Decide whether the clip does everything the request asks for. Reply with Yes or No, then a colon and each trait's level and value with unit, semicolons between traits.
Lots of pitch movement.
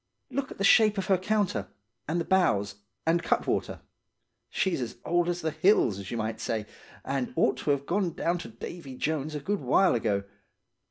Yes: wide, 7.9 semitones